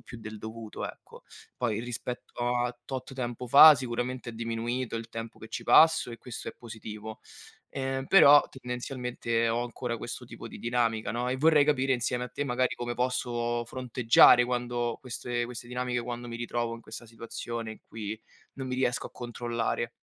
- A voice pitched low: Yes, low, 120 Hz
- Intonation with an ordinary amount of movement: No, narrow, 1.5 semitones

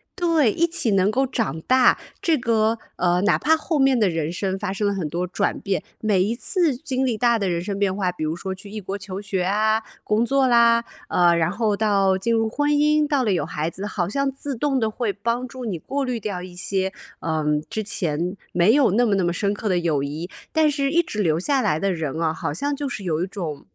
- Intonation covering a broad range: Yes, wide, 5.8 semitones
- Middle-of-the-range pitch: No, high, 205 Hz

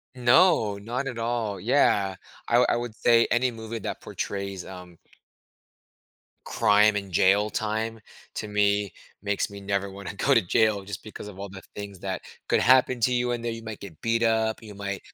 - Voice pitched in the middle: No, low, 105 Hz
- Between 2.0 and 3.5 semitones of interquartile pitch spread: Yes, narrow, 2.6 semitones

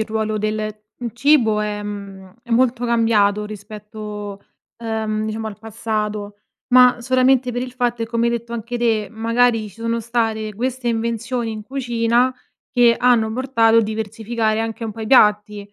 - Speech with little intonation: Yes, narrow, 2.0 semitones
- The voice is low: No, high, 225 Hz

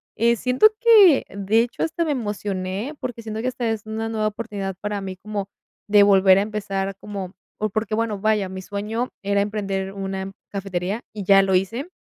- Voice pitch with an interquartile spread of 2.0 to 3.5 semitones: Yes, narrow, 2.6 semitones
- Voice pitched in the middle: No, high, 205 Hz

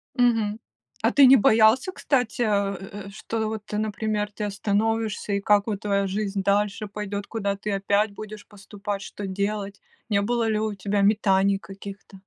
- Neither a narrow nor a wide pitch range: No, narrow, 1.5 semitones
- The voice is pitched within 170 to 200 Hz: No, high, 210 Hz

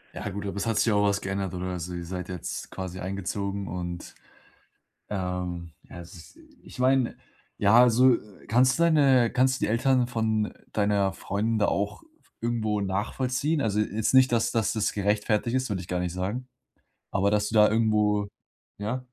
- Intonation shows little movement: No, average, 3.7 semitones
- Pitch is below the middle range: Yes, low, 105 Hz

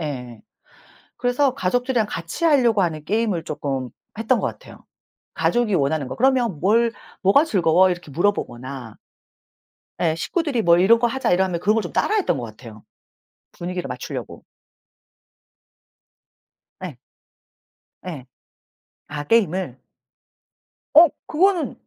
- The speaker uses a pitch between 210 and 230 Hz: No, medium, 185 Hz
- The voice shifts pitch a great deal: Yes, wide, 7.6 semitones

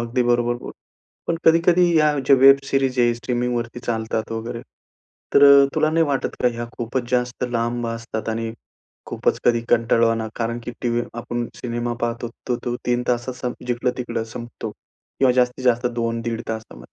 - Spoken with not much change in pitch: Yes, narrow, 1.4 semitones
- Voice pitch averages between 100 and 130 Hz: Yes, low, 120 Hz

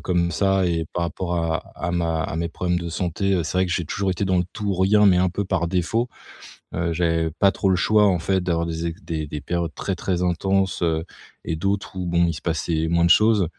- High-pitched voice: No, very low, 85 Hz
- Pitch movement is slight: Yes, narrow, 2.3 semitones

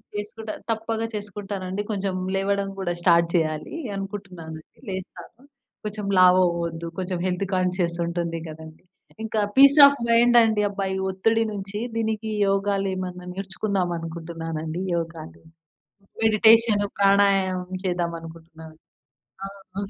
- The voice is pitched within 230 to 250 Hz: No, high, 190 Hz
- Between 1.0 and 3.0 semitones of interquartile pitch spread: No, average, 3.4 semitones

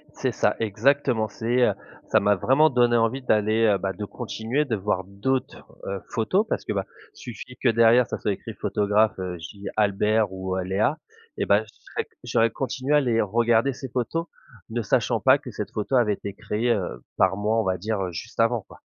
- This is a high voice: No, low, 110 Hz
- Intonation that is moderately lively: Yes, average, 3.4 semitones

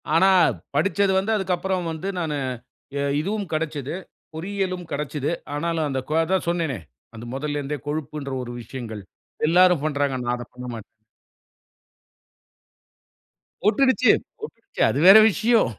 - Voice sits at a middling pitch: Yes, medium, 160 Hz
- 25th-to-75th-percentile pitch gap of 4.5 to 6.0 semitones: Yes, average, 5.2 semitones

